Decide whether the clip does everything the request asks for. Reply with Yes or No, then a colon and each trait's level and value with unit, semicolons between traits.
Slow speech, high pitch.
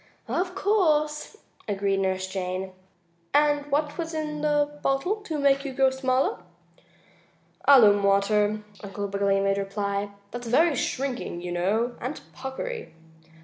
Yes: slow, 130 wpm; very high, 255 Hz